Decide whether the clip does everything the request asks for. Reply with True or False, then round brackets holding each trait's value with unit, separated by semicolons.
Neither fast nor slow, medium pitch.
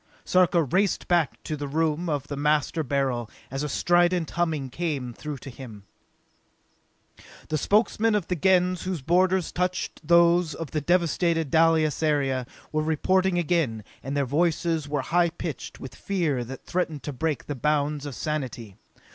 True (160 wpm; 155 Hz)